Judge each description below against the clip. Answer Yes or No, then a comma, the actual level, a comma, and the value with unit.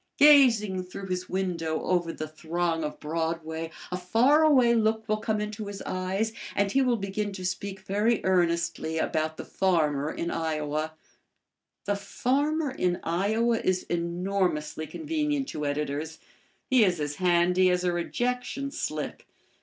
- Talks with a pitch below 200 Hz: Yes, medium, 185 Hz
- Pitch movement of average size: Yes, average, 5.0 semitones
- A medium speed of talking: Yes, average, 145 wpm